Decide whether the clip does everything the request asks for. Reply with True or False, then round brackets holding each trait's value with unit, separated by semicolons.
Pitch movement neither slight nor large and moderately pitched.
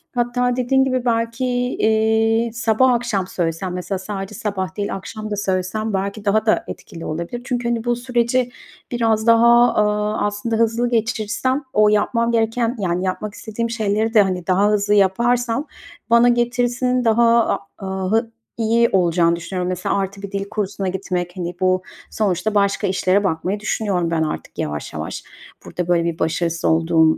False (3.9 semitones; 210 Hz)